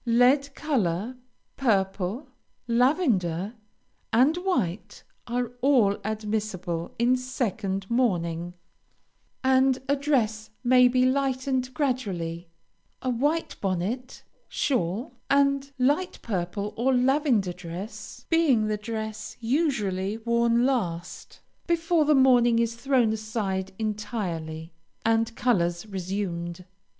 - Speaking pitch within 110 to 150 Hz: No, high, 230 Hz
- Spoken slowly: Yes, slow, 100 wpm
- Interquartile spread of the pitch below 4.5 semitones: No, average, 5.2 semitones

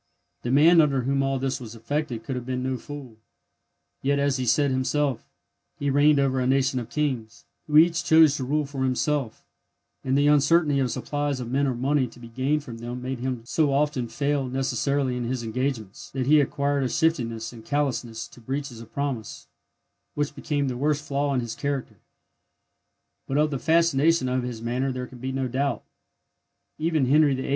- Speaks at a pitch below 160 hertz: Yes, low, 135 Hz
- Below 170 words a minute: No, average, 195 wpm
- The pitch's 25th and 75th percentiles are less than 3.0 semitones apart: Yes, narrow, 2.6 semitones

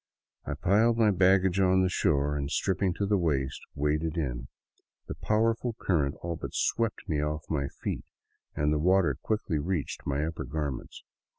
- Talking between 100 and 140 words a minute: No, average, 170 wpm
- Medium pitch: No, very low, 80 Hz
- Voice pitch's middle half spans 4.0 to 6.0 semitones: Yes, average, 4.8 semitones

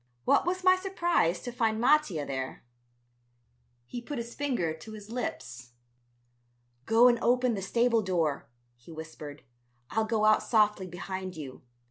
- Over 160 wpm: No, average, 145 wpm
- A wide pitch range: Yes, wide, 7.2 semitones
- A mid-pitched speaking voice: No, high, 215 Hz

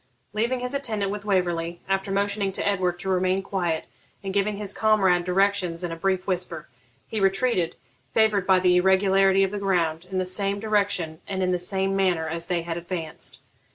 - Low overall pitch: No, high, 190 Hz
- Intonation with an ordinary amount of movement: No, narrow, 2.1 semitones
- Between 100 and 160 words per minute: No, average, 190 wpm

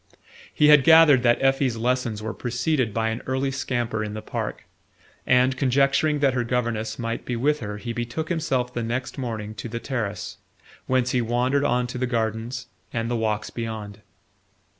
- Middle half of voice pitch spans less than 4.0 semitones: Yes, average, 2.7 semitones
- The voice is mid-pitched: No, low, 120 Hz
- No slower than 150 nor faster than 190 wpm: Yes, average, 180 wpm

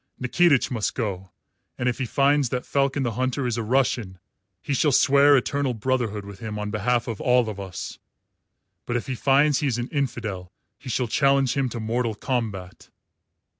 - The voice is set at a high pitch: No, low, 125 Hz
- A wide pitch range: No, average, 3.9 semitones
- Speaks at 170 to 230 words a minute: Yes, average, 185 wpm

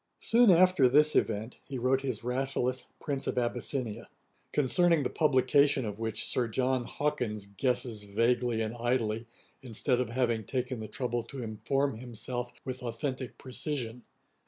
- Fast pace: No, average, 150 wpm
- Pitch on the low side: Yes, low, 125 Hz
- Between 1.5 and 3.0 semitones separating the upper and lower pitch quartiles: Yes, average, 2.7 semitones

